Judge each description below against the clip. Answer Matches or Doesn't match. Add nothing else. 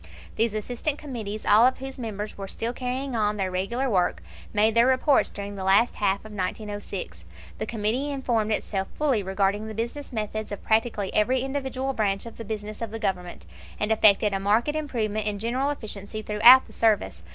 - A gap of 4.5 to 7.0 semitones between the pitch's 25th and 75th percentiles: Doesn't match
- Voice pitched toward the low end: Doesn't match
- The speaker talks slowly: Doesn't match